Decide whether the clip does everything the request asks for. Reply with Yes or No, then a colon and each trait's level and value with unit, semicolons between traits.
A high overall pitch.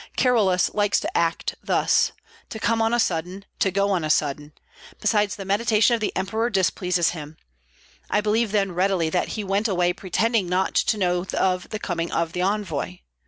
Yes: high, 195 Hz